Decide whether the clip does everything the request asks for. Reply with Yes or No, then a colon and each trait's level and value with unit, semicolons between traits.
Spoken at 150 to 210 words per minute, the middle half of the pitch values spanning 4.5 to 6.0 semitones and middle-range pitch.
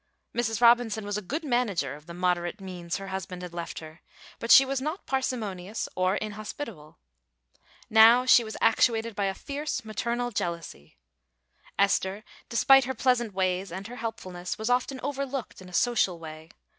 No: average, 165 wpm; average, 5.0 semitones; high, 215 Hz